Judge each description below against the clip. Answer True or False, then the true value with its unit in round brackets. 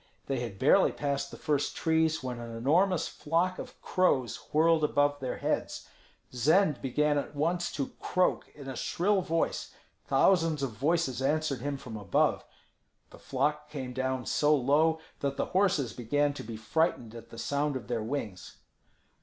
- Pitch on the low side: False (145 Hz)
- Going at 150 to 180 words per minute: True (165 wpm)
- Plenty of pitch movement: False (4.1 semitones)